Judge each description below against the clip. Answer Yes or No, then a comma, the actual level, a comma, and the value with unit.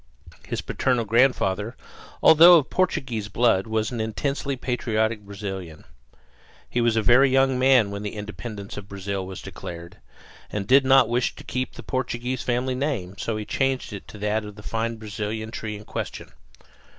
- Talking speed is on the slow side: No, average, 170 wpm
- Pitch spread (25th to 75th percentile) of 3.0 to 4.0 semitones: Yes, average, 3.7 semitones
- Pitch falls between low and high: No, low, 110 Hz